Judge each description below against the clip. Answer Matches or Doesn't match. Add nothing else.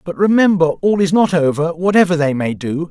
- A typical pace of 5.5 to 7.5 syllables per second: Matches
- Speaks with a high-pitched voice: Doesn't match